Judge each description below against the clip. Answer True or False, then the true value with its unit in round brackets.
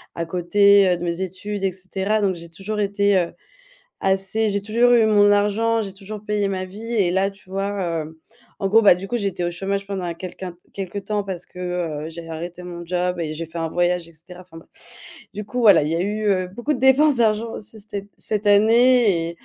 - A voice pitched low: False (195 Hz)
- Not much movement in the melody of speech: False (3.0 semitones)